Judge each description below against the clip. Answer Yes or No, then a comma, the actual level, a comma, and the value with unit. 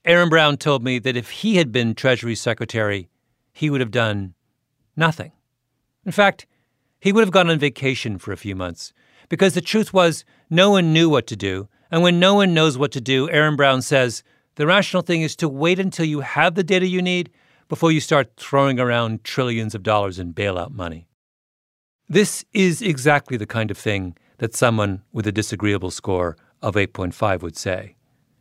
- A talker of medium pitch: No, low, 130 Hz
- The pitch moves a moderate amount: No, wide, 7.2 semitones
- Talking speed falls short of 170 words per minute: No, average, 190 wpm